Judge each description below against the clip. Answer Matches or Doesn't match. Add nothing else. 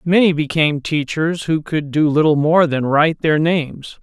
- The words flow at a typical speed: Matches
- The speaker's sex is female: Doesn't match